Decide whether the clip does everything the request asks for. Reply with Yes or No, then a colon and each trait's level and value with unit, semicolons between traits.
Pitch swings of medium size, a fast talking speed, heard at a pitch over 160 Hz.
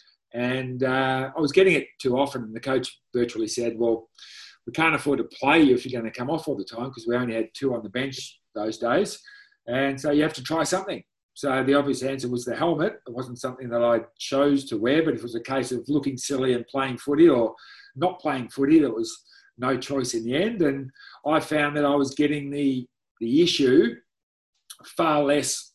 No: average, 3.4 semitones; fast, 225 wpm; low, 135 Hz